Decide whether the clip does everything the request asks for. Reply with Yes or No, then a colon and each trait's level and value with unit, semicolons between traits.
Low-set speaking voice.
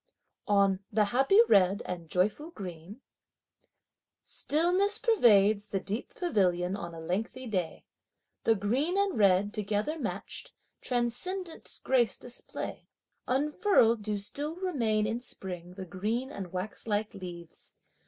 No: high, 215 Hz